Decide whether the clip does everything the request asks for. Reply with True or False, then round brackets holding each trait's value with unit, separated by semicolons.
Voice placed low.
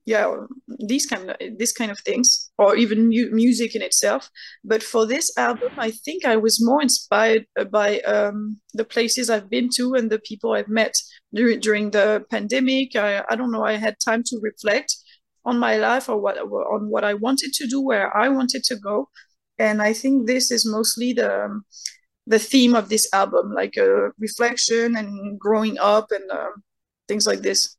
False (230 Hz)